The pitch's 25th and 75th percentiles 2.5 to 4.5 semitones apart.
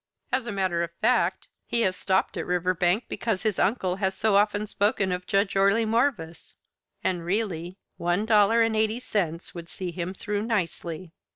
Yes: average, 3.4 semitones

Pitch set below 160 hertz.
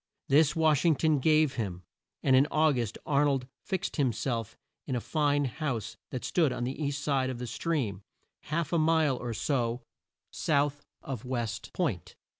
Yes: medium, 140 Hz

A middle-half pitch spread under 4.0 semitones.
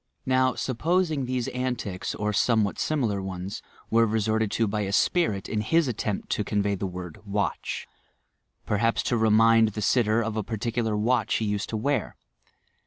Yes: average, 3.1 semitones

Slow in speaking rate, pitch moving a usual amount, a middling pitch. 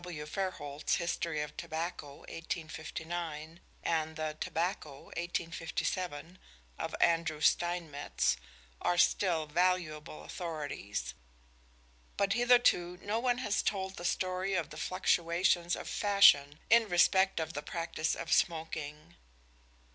Yes: slow, 110 wpm; average, 3.0 semitones; medium, 170 Hz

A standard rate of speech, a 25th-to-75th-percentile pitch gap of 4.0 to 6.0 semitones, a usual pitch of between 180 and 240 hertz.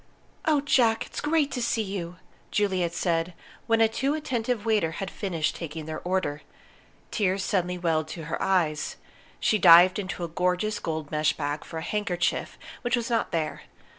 Yes: average, 170 wpm; average, 5.2 semitones; medium, 185 Hz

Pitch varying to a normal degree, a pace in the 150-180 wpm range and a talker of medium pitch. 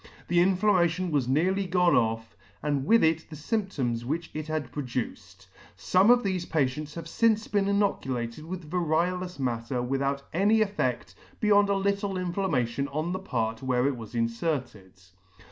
No: wide, 6.7 semitones; average, 160 wpm; medium, 155 Hz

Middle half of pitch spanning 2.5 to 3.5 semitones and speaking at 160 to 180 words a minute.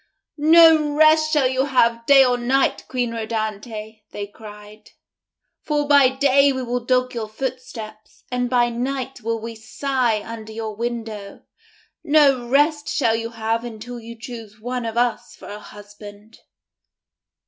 No: average, 3.2 semitones; average, 150 wpm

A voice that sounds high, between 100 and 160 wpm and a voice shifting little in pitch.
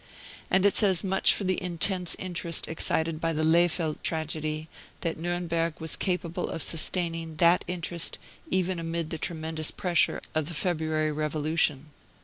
No: medium, 165 Hz; average, 145 wpm; narrow, 1.9 semitones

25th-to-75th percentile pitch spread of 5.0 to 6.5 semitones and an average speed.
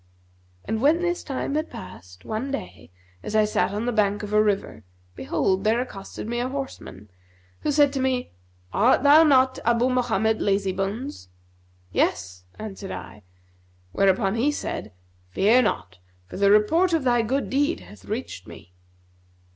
Yes: average, 5.3 semitones; average, 155 wpm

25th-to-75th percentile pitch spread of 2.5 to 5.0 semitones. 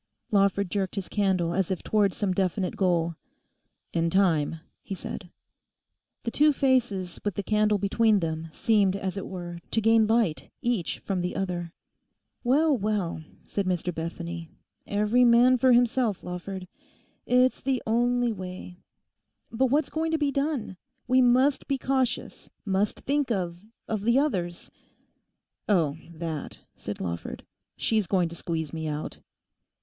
No: wide, 5.4 semitones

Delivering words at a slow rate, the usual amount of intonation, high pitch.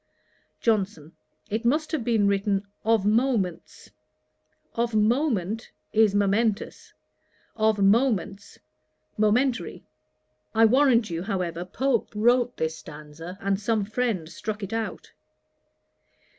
Yes: slow, 105 wpm; average, 3.1 semitones; high, 215 Hz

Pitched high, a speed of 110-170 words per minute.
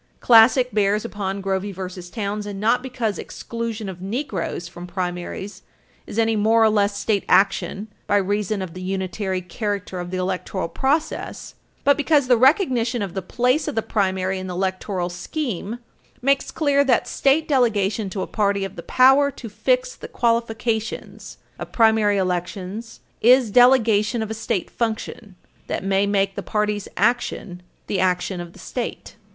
Yes: high, 210 Hz; average, 160 wpm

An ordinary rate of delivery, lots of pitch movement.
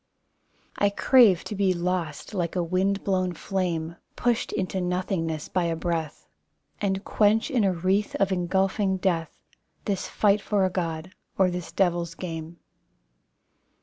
No: average, 145 wpm; narrow, 2.5 semitones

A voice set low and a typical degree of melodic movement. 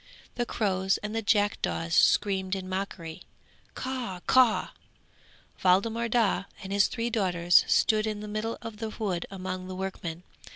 No: high, 200 Hz; average, 3.1 semitones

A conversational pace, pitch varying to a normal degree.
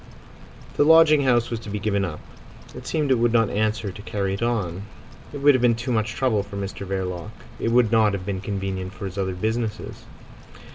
No: fast, 210 wpm; average, 3.6 semitones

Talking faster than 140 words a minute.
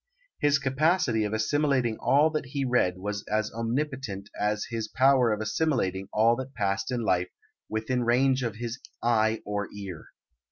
Yes: average, 160 wpm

